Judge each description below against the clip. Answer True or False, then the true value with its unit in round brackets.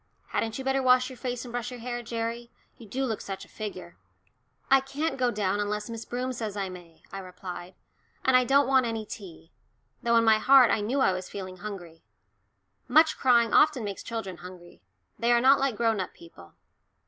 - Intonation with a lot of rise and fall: False (4.5 semitones)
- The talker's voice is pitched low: False (230 Hz)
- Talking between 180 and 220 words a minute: True (205 wpm)